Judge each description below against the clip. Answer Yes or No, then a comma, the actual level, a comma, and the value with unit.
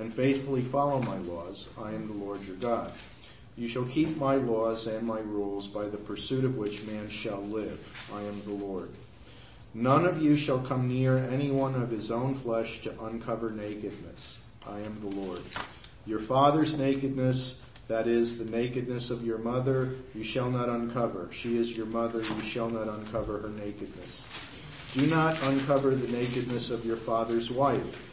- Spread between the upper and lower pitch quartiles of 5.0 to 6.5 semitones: No, average, 3.2 semitones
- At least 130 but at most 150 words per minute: No, average, 175 wpm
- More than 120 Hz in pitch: No, low, 115 Hz